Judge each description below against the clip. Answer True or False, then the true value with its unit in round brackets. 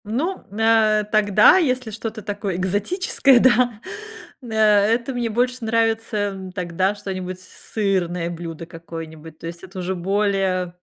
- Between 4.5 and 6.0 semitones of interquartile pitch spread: False (3.6 semitones)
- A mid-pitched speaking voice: False (205 Hz)